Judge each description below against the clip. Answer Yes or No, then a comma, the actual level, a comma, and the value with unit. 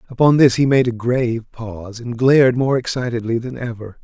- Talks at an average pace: Yes, average, 195 wpm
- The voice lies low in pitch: Yes, low, 120 Hz